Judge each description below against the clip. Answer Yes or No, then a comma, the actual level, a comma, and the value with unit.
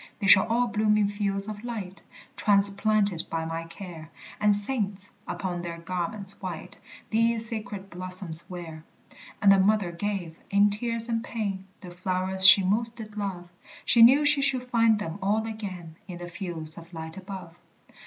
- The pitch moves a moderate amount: Yes, average, 3.4 semitones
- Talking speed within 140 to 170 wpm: Yes, average, 165 wpm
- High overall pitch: Yes, high, 200 Hz